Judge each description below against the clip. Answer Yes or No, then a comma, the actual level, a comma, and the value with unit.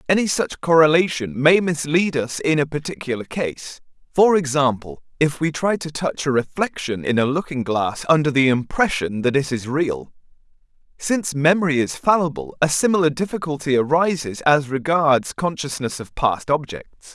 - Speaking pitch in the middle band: Yes, medium, 145 Hz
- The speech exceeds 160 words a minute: No, average, 155 wpm